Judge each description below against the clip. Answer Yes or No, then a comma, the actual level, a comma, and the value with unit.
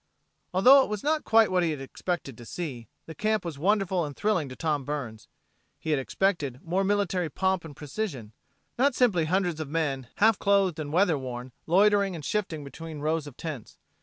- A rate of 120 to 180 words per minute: No, average, 195 wpm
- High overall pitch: No, medium, 165 Hz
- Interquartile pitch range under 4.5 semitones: No, wide, 5.4 semitones